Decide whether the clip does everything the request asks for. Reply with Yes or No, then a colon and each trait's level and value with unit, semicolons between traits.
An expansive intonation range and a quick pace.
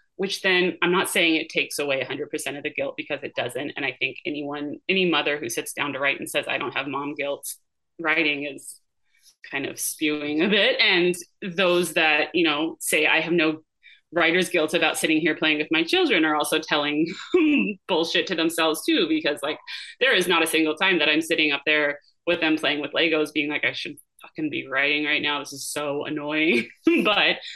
No: average, 3.5 semitones; fast, 210 wpm